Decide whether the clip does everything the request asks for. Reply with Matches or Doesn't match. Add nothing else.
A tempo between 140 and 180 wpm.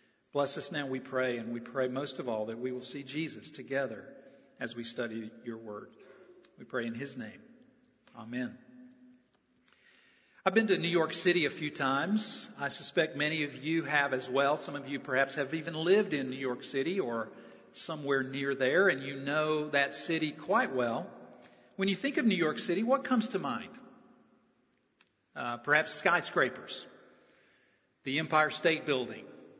Matches